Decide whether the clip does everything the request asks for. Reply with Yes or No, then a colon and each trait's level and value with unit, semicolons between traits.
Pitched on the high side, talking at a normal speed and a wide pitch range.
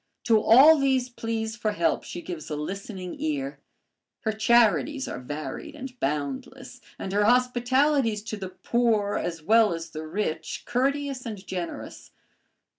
Yes: high, 220 Hz; average, 145 wpm; wide, 5.8 semitones